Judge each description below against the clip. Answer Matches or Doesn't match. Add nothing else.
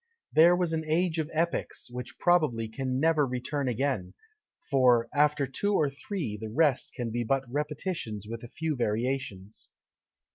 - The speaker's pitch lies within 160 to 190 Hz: Doesn't match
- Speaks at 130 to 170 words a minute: Matches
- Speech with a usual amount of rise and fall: Matches